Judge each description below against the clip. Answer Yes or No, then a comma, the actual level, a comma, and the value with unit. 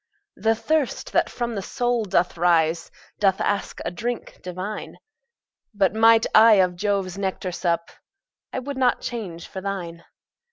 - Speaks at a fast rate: No, average, 150 wpm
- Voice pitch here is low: No, high, 195 Hz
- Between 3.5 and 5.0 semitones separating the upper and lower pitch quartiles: Yes, average, 4.2 semitones